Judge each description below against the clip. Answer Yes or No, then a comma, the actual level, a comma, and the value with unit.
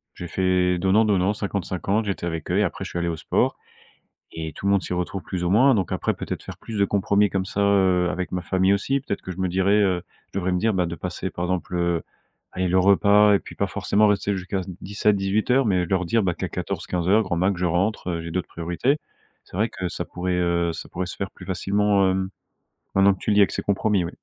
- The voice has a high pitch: No, very low, 95 Hz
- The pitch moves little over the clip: Yes, narrow, 2.2 semitones